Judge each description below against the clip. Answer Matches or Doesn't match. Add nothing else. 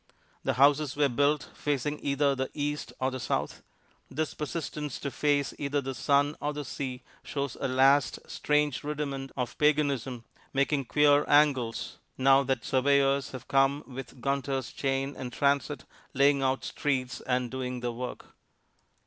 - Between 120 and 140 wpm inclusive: Doesn't match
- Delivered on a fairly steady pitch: Matches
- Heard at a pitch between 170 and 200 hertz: Doesn't match